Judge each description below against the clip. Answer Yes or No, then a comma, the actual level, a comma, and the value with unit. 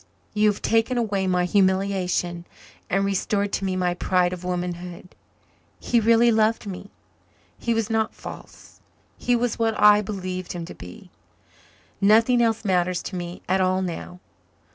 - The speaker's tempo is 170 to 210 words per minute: No, average, 155 wpm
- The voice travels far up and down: No, average, 3.4 semitones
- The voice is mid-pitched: No, high, 195 Hz